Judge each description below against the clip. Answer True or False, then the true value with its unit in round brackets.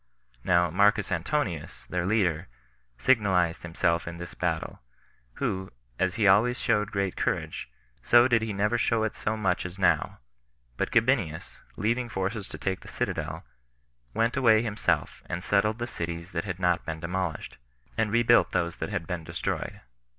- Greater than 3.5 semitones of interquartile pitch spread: True (4.1 semitones)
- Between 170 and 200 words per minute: False (160 wpm)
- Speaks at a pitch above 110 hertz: False (95 Hz)